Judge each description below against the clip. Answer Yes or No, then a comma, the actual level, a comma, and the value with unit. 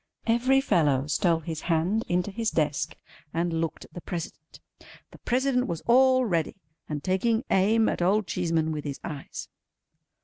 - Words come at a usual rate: Yes, average, 160 wpm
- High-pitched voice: No, medium, 175 Hz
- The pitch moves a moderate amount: No, wide, 6.1 semitones